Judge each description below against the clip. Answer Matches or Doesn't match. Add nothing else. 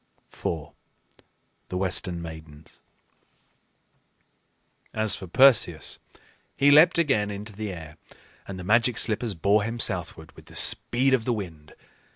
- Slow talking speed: Matches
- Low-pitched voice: Matches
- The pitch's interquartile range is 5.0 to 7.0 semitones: Matches